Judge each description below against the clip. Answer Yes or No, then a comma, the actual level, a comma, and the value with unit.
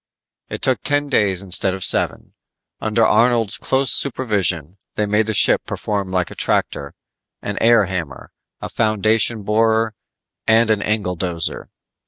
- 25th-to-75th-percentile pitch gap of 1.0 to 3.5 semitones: Yes, average, 3.1 semitones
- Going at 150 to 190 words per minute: No, average, 140 wpm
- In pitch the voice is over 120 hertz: No, low, 105 Hz